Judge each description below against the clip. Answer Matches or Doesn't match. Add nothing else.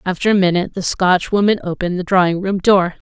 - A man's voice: Doesn't match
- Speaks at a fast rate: Doesn't match